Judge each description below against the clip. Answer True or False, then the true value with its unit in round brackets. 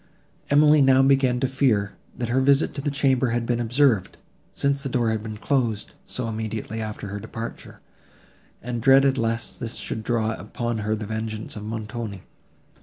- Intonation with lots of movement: False (3.4 semitones)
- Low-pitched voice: True (115 Hz)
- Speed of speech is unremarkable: True (175 wpm)